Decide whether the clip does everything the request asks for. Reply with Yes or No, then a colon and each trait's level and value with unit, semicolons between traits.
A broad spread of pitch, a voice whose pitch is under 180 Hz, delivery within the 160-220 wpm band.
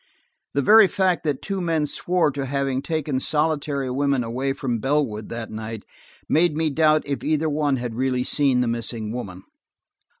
No: average, 3.7 semitones; medium, 140 Hz; average, 170 wpm